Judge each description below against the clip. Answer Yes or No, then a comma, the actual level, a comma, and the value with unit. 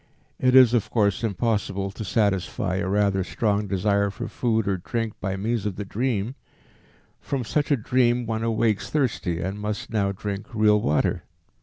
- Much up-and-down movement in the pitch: No, average, 2.8 semitones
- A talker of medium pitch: No, low, 105 Hz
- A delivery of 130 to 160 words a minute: No, average, 170 wpm